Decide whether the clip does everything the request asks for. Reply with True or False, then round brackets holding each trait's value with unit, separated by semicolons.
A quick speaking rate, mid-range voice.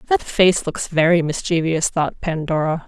False (145 wpm; 170 Hz)